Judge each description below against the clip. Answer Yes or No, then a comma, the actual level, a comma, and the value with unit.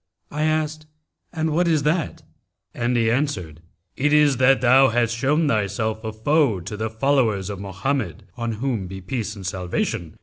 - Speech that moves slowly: No, average, 170 wpm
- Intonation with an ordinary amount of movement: No, wide, 5.8 semitones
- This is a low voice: Yes, low, 120 Hz